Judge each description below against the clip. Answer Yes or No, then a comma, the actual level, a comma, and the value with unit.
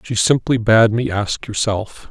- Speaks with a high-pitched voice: No, low, 110 Hz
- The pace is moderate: Yes, average, 170 wpm